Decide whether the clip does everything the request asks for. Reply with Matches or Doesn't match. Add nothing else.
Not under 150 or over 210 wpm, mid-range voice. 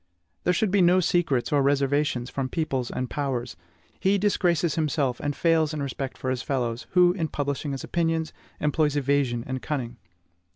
Matches